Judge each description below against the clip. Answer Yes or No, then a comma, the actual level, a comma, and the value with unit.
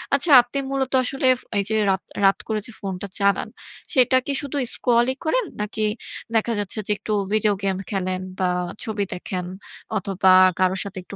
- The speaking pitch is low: No, high, 210 Hz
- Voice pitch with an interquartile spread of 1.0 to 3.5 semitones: No, average, 4.5 semitones